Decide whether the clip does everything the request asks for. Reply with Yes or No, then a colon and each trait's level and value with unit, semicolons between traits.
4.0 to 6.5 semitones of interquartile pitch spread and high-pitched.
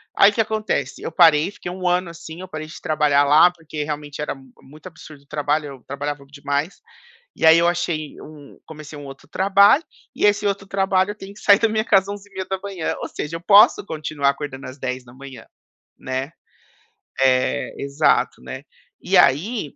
No: average, 5.1 semitones; medium, 155 Hz